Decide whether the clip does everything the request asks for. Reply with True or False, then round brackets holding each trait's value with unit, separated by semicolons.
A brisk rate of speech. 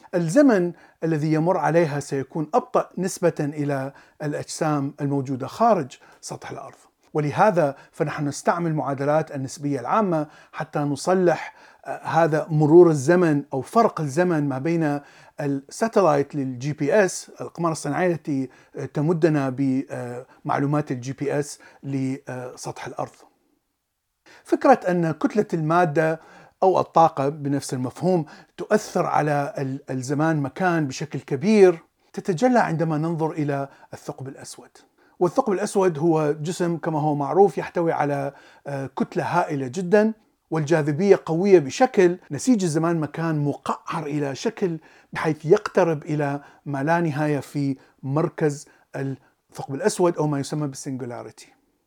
False (115 wpm)